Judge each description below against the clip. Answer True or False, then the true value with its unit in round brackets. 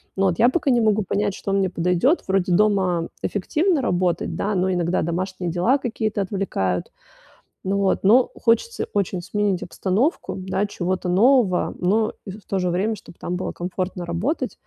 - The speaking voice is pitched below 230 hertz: True (190 Hz)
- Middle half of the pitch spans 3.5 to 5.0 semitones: False (3.1 semitones)